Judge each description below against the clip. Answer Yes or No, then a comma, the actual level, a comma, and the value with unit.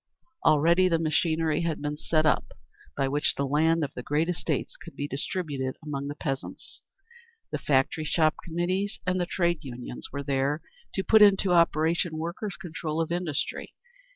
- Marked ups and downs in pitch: No, average, 3.1 semitones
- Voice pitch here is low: No, medium, 160 Hz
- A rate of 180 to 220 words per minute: No, average, 165 wpm